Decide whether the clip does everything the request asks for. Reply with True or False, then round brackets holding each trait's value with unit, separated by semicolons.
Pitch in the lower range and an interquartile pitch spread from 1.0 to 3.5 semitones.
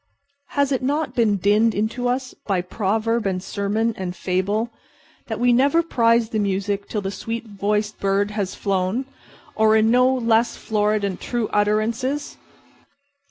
False (220 Hz; 2.9 semitones)